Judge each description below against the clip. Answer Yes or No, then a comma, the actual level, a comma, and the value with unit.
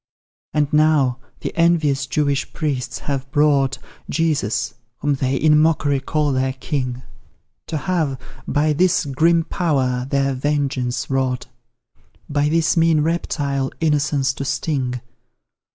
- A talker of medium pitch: Yes, medium, 145 Hz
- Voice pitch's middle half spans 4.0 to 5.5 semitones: No, average, 2.7 semitones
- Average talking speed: No, slow, 120 wpm